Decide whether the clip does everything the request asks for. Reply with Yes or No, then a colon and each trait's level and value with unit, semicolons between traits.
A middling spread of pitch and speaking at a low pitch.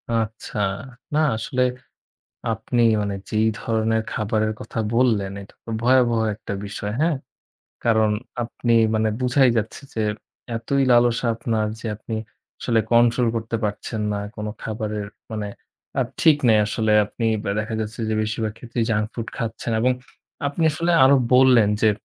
No: narrow, 1.9 semitones; low, 115 Hz